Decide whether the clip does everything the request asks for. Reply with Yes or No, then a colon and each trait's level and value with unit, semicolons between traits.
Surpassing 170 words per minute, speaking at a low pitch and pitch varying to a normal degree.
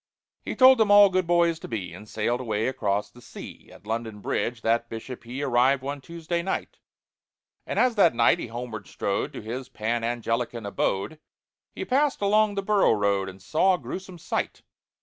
No: average, 190 wpm; low, 125 Hz; wide, 7.7 semitones